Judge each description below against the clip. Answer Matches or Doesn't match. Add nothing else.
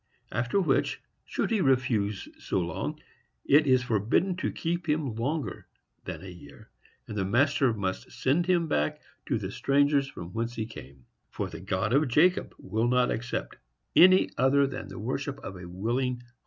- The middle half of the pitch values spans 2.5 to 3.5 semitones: Doesn't match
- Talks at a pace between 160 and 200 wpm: Matches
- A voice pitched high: Doesn't match